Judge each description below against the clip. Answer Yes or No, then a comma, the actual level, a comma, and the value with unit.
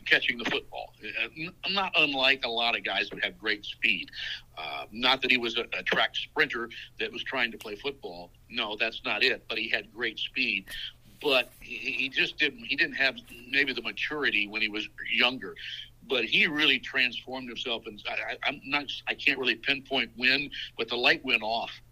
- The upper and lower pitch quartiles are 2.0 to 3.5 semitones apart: Yes, average, 2.8 semitones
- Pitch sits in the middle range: No, low, 125 Hz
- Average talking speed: Yes, average, 190 wpm